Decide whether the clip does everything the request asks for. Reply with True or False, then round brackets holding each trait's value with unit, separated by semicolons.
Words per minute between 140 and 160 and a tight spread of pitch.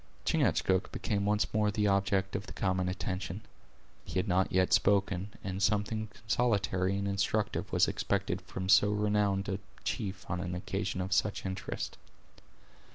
True (155 wpm; 1.7 semitones)